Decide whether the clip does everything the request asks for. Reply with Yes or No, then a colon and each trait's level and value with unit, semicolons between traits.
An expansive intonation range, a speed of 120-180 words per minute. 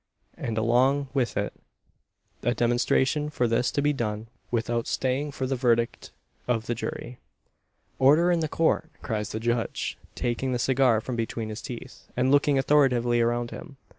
No: average, 2.7 semitones; average, 165 wpm